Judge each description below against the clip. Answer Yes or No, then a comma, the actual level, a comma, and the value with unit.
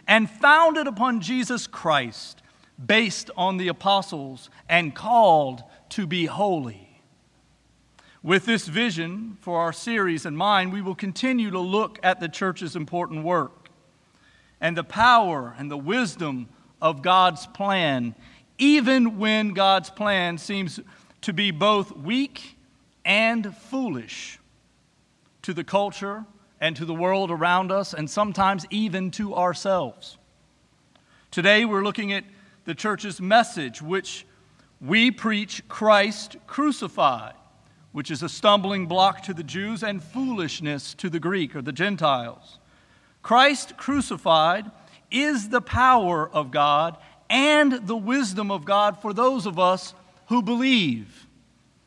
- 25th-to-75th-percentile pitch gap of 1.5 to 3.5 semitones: No, average, 4.4 semitones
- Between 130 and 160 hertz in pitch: No, high, 195 Hz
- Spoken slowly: Yes, slow, 130 wpm